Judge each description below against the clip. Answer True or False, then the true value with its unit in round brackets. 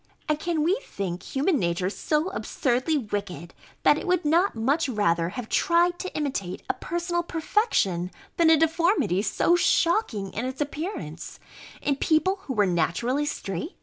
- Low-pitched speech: False (290 Hz)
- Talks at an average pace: True (155 wpm)